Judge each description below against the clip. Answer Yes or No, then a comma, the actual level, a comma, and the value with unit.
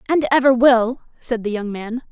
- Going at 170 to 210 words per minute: Yes, average, 200 wpm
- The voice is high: Yes, high, 240 Hz